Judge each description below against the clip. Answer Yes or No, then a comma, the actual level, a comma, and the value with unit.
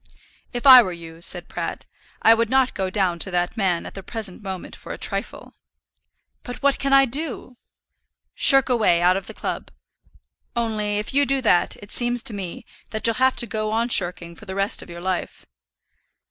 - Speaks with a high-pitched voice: Yes, high, 215 Hz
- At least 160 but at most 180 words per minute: No, average, 200 wpm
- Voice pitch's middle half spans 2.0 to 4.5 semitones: No, average, 4.9 semitones